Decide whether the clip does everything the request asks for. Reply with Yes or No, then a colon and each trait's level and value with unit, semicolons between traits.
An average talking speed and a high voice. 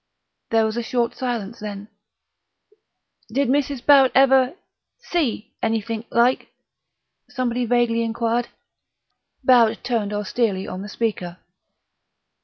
No: slow, 105 wpm; high, 235 Hz